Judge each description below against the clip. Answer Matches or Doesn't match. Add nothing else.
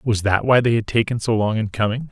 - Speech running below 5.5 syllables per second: Doesn't match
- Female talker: Doesn't match